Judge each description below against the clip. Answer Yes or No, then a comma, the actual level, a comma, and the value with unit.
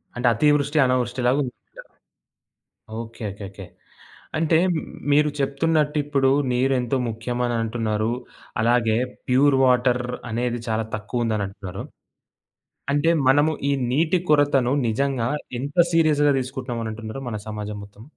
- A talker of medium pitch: No, low, 125 Hz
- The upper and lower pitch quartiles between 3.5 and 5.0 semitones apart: Yes, average, 4.1 semitones